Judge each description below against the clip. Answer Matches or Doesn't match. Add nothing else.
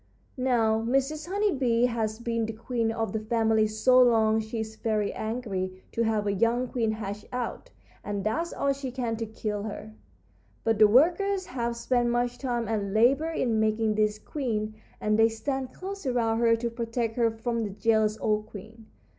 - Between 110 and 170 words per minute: Doesn't match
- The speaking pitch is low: Doesn't match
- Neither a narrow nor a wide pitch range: Doesn't match